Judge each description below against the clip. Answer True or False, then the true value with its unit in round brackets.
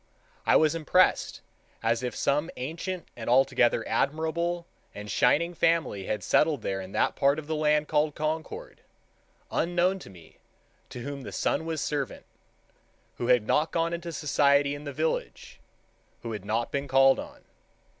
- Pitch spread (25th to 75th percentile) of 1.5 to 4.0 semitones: False (4.6 semitones)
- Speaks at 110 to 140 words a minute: False (150 wpm)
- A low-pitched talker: False (145 Hz)